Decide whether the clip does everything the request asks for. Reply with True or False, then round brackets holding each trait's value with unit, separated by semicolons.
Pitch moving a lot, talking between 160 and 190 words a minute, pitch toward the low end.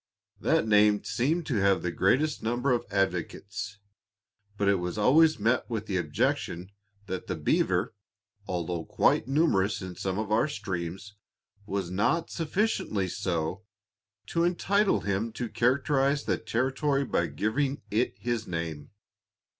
False (6.1 semitones; 140 wpm; 105 Hz)